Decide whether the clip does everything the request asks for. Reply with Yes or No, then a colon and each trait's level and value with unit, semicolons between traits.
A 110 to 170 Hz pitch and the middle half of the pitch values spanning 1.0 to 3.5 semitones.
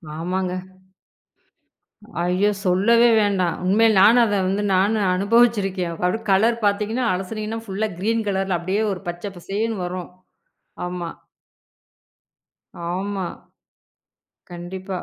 No: high, 195 Hz; average, 3.0 semitones